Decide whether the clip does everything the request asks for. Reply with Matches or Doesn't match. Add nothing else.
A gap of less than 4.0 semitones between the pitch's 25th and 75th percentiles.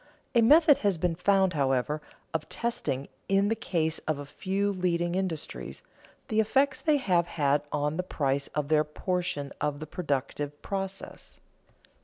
Doesn't match